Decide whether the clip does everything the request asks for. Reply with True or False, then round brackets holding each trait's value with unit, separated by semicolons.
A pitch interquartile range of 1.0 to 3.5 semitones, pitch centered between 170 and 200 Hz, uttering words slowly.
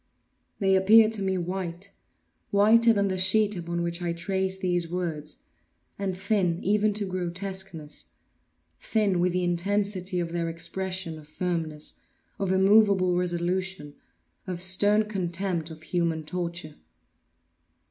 True (2.4 semitones; 185 Hz; 115 wpm)